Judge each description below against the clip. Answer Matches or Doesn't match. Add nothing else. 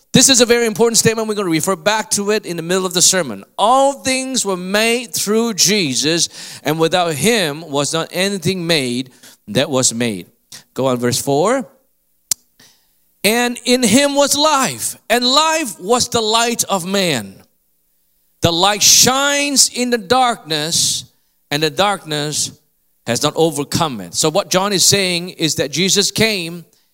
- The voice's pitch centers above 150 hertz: Matches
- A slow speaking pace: Doesn't match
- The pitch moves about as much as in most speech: Doesn't match